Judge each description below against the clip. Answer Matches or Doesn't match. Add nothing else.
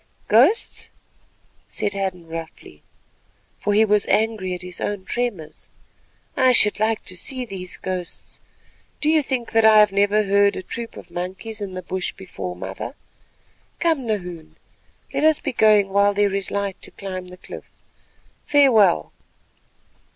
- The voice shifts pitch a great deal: Doesn't match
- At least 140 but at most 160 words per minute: Matches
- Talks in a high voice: Matches